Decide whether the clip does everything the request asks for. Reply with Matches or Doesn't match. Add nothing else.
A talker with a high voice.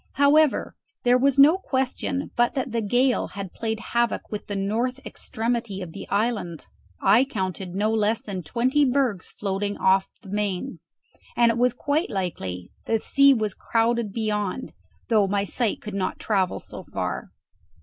Matches